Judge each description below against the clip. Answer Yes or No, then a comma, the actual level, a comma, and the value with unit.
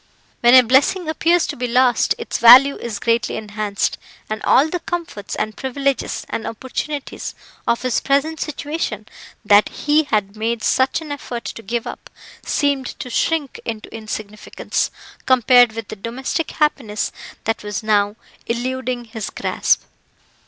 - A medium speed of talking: Yes, average, 145 wpm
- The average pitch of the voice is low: No, high, 240 Hz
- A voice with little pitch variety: No, average, 4.2 semitones